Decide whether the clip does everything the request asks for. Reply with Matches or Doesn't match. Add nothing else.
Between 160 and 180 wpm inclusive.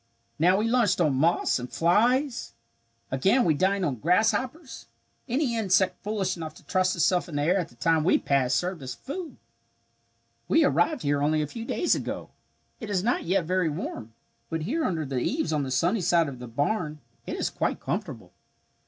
Doesn't match